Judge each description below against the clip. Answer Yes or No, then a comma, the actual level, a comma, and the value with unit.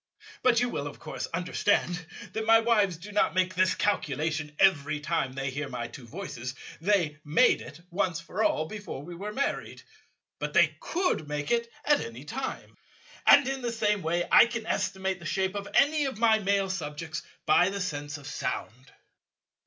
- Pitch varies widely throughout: Yes, wide, 6.1 semitones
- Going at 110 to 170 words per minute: No, average, 185 wpm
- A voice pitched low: No, medium, 185 Hz